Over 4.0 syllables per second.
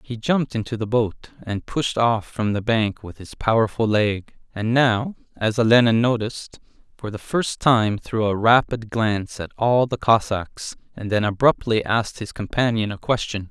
Yes: 4.6 syllables/s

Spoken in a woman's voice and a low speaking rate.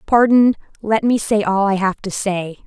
No: female; average, 200 wpm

